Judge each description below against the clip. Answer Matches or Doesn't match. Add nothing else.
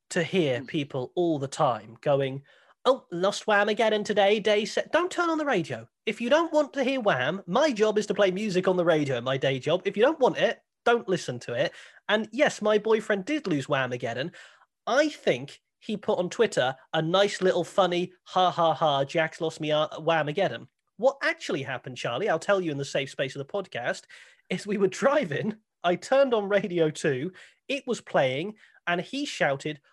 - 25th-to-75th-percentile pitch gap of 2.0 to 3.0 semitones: Doesn't match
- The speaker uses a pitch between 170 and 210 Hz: Matches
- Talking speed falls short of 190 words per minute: Doesn't match